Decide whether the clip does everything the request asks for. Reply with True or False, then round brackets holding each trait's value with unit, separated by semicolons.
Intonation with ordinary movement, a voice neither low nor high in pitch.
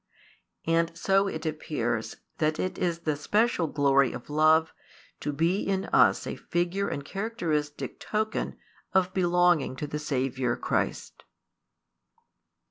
True (3.9 semitones; 160 Hz)